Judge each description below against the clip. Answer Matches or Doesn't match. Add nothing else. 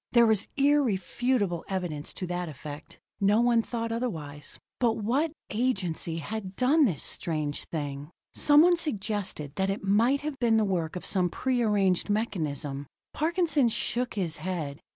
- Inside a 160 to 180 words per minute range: Doesn't match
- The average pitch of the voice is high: Matches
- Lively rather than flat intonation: Matches